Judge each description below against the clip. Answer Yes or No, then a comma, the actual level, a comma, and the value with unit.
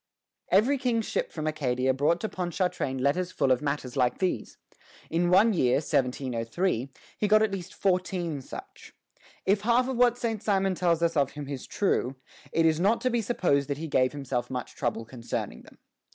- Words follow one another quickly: No, average, 185 wpm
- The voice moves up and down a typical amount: No, wide, 6.9 semitones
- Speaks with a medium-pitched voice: Yes, medium, 170 Hz